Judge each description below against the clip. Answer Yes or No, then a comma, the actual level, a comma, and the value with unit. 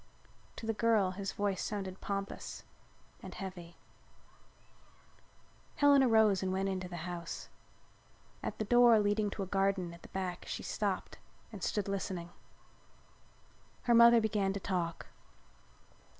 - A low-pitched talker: No, high, 195 Hz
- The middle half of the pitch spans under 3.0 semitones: Yes, narrow, 2.6 semitones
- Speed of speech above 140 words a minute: No, slow, 135 wpm